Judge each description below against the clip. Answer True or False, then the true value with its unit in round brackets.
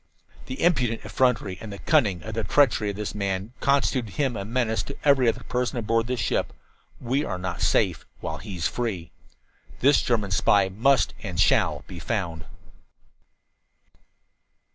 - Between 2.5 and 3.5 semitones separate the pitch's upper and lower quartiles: False (4.5 semitones)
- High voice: False (115 Hz)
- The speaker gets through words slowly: False (150 wpm)